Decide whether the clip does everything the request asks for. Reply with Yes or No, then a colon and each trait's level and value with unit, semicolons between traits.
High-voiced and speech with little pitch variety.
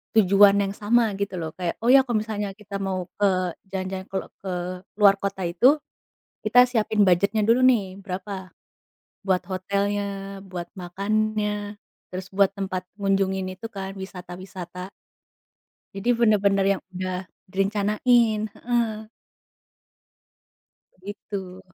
Yes: high, 195 Hz; narrow, 2.0 semitones